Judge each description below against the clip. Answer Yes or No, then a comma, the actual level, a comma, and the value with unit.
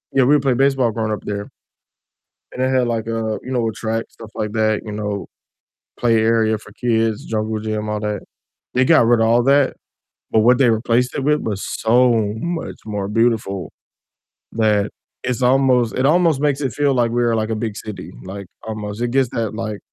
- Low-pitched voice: Yes, low, 115 Hz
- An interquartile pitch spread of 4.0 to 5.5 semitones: No, average, 2.8 semitones